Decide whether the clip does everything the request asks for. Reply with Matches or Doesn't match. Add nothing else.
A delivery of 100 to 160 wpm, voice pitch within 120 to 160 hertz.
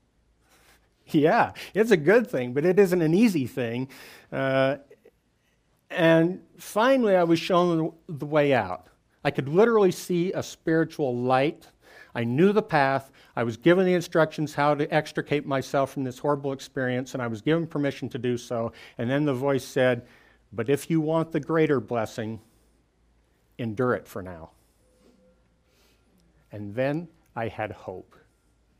Matches